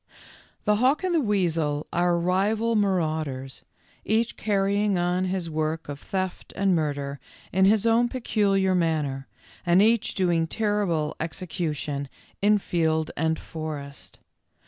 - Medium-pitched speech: Yes, medium, 180 Hz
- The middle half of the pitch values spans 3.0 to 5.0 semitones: Yes, average, 4.6 semitones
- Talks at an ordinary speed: No, slow, 130 wpm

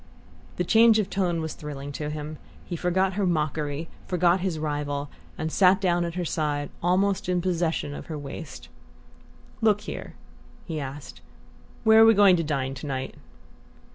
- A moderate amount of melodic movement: Yes, average, 4.0 semitones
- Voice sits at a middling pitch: Yes, medium, 165 Hz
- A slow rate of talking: No, average, 170 wpm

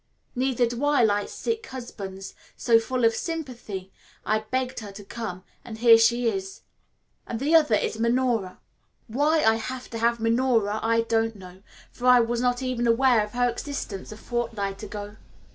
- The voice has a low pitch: No, high, 235 Hz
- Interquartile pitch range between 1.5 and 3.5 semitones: Yes, average, 2.7 semitones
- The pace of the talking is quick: No, average, 175 wpm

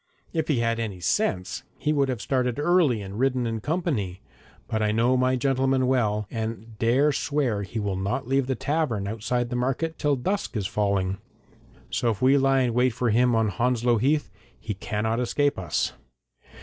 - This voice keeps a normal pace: Yes, average, 185 wpm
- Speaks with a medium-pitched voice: No, low, 120 Hz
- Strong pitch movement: No, average, 3.8 semitones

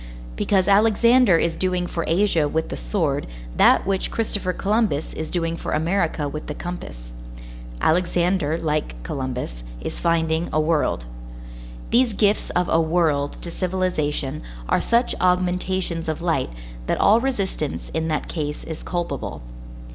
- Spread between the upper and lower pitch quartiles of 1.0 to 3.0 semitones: No, average, 3.5 semitones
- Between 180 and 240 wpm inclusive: No, average, 140 wpm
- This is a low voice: No, medium, 170 Hz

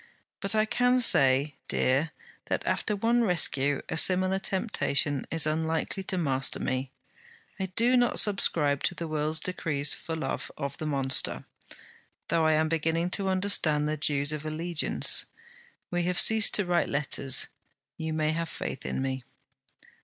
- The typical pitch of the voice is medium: Yes, medium, 160 Hz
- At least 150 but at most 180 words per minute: Yes, average, 155 wpm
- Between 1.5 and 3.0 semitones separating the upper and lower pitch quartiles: No, average, 4.4 semitones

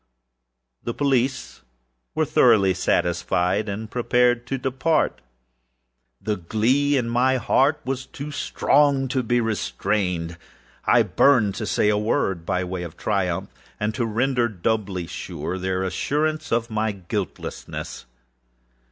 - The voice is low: Yes, low, 110 Hz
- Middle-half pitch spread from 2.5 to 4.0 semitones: No, wide, 5.6 semitones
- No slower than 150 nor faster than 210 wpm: No, slow, 135 wpm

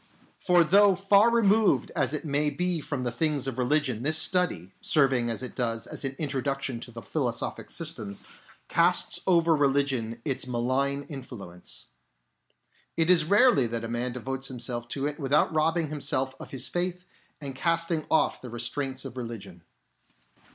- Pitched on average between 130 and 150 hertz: Yes, medium, 140 Hz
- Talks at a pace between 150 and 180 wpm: Yes, average, 165 wpm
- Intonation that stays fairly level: No, average, 4.8 semitones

